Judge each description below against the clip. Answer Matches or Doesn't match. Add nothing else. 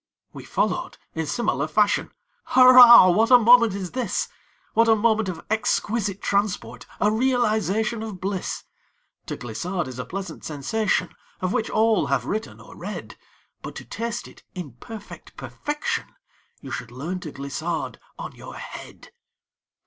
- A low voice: Doesn't match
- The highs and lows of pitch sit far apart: Doesn't match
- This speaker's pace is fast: Doesn't match